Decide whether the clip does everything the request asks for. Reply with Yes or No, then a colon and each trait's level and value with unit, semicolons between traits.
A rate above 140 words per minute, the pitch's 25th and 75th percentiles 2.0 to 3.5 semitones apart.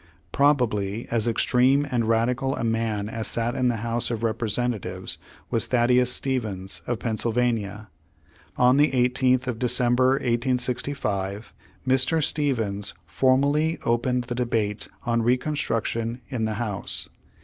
No: slow, 135 wpm; narrow, 2.4 semitones